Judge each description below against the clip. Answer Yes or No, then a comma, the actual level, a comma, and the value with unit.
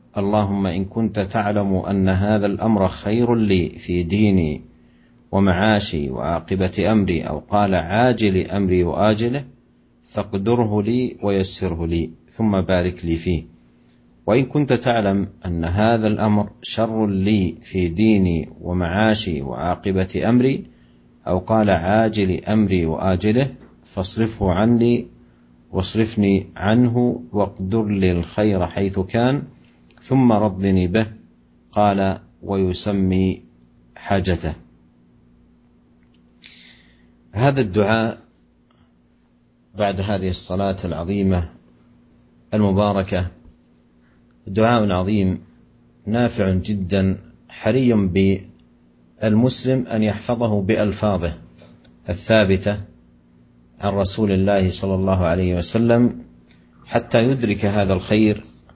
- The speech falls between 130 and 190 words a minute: No, slow, 90 wpm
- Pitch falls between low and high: No, very low, 95 Hz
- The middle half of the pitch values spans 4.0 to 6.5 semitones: Yes, average, 4.9 semitones